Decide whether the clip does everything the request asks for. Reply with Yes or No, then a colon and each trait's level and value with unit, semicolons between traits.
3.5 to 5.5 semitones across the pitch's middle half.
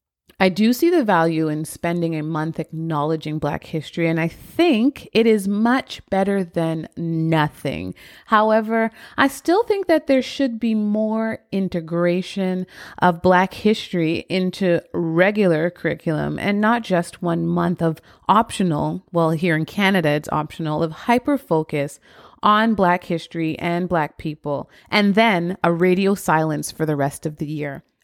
Yes: average, 4.7 semitones